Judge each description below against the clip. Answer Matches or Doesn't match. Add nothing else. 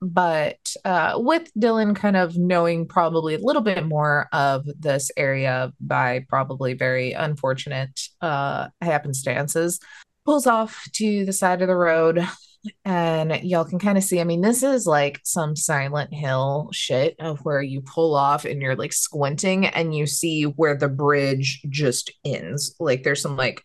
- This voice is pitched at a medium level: Matches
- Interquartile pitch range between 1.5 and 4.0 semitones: Doesn't match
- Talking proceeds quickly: Doesn't match